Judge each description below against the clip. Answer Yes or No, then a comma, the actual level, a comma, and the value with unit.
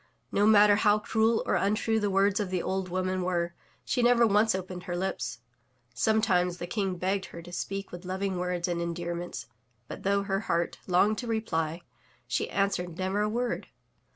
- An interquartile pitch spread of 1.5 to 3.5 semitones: Yes, average, 2.8 semitones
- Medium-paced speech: Yes, average, 180 wpm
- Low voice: No, high, 190 Hz